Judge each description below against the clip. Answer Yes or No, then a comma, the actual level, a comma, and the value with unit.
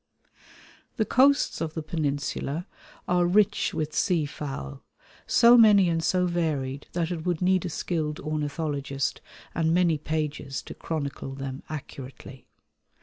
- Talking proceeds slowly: Yes, slow, 130 wpm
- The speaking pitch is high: No, medium, 155 Hz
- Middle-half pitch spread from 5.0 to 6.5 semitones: No, average, 3.8 semitones